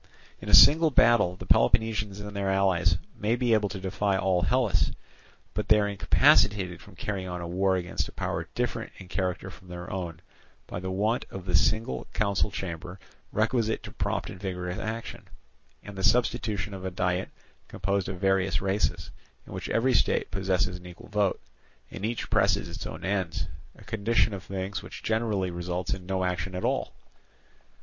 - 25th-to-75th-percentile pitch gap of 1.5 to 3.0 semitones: Yes, narrow, 2.5 semitones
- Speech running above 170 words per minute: Yes, average, 180 wpm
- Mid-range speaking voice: No, very low, 95 Hz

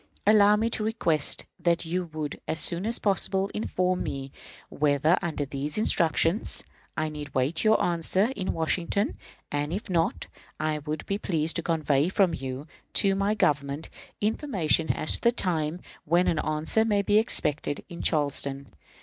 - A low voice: No, medium, 165 Hz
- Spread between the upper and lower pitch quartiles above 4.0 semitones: Yes, average, 4.7 semitones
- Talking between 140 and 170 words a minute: Yes, average, 160 wpm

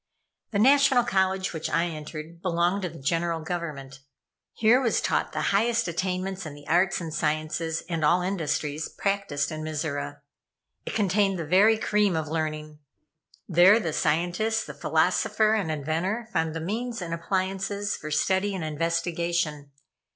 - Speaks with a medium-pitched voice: Yes, medium, 175 Hz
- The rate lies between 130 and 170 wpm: Yes, average, 150 wpm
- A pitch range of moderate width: Yes, average, 3.9 semitones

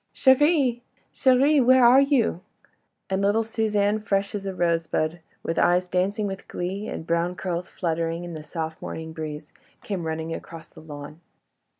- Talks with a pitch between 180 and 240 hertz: Yes, medium, 185 Hz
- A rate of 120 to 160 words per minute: Yes, average, 155 wpm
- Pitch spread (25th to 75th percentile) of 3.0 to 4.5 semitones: No, average, 4.9 semitones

